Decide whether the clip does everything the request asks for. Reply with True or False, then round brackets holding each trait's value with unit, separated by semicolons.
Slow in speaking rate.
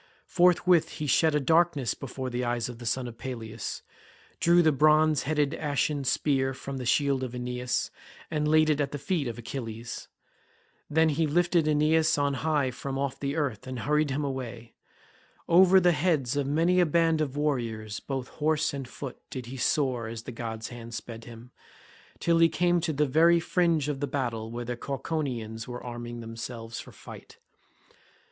False (180 wpm)